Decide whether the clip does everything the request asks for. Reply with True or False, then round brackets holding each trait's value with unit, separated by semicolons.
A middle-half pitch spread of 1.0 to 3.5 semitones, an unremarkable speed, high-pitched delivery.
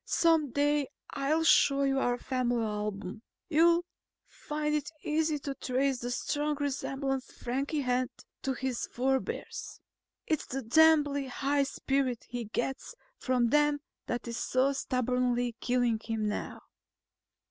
False (3.1 semitones; 130 wpm; 270 Hz)